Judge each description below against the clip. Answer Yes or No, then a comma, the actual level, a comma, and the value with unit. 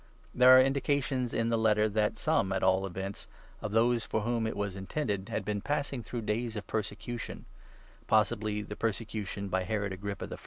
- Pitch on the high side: No, low, 110 Hz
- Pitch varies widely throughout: No, average, 2.8 semitones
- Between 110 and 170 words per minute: No, average, 190 wpm